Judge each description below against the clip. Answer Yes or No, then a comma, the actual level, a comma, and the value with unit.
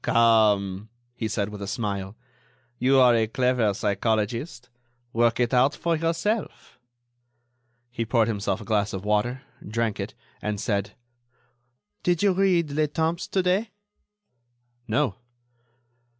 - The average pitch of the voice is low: Yes, low, 115 Hz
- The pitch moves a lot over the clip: Yes, wide, 5.9 semitones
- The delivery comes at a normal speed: No, slow, 130 wpm